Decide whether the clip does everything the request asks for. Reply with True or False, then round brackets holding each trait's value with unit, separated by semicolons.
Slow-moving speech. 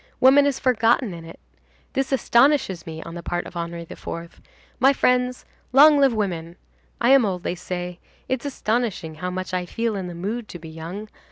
False (190 wpm)